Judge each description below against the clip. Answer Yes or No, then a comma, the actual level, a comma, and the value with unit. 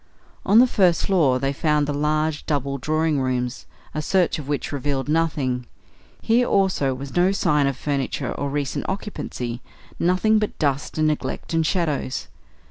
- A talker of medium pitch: Yes, medium, 150 Hz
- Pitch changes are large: No, average, 4.0 semitones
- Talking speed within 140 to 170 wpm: Yes, average, 160 wpm